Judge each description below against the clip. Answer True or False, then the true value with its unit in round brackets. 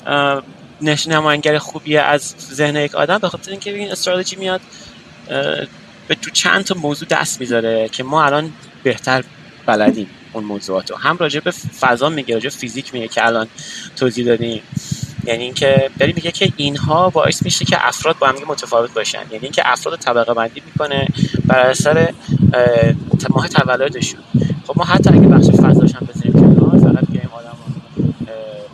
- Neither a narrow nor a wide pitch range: True (4.6 semitones)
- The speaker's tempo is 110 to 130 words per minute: False (145 wpm)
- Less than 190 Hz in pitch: True (140 Hz)